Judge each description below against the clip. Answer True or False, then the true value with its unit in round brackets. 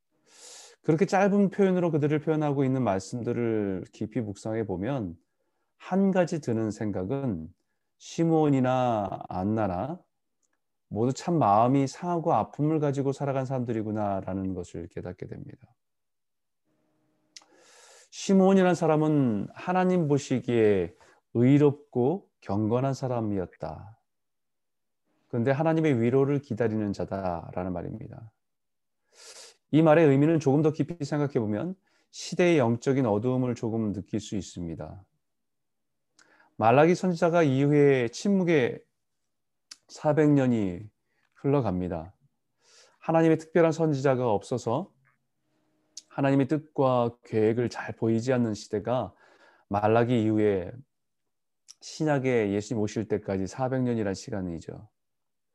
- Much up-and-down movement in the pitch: True (6.1 semitones)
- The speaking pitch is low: True (125 Hz)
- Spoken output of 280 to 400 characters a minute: False (255 characters per minute)